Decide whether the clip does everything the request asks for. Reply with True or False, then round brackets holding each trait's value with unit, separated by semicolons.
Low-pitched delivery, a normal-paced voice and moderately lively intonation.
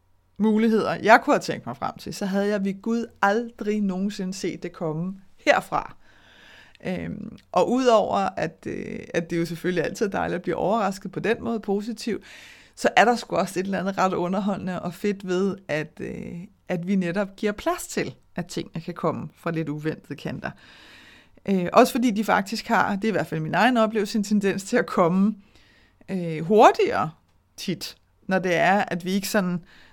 False (195 Hz; 190 wpm; 3.6 semitones)